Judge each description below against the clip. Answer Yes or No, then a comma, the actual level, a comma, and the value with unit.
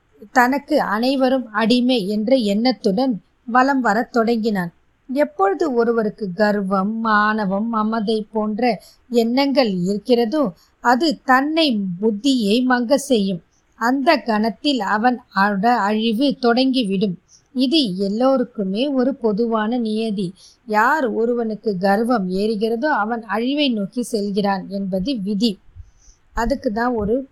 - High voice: Yes, high, 230 Hz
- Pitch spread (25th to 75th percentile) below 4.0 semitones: Yes, average, 3.5 semitones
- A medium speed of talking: Yes, average, 95 wpm